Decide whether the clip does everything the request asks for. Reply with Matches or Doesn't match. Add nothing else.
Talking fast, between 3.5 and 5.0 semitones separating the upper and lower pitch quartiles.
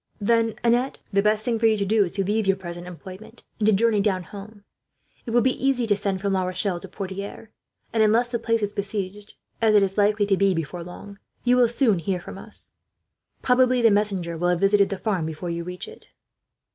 Doesn't match